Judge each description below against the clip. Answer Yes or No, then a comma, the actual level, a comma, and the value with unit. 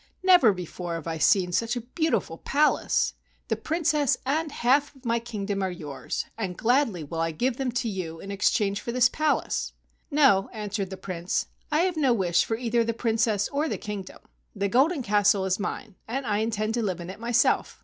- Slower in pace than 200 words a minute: No, fast, 205 wpm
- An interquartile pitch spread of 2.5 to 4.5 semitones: No, average, 5.0 semitones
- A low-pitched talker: No, high, 220 Hz